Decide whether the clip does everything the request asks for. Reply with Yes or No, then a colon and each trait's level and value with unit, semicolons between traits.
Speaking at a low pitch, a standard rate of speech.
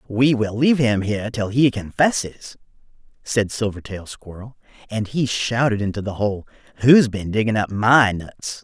Yes: low, 110 Hz; average, 155 wpm